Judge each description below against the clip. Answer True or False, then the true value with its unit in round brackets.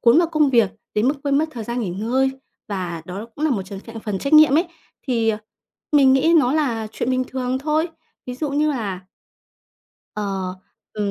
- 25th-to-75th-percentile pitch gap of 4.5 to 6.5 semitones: True (5.5 semitones)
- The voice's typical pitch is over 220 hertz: True (250 Hz)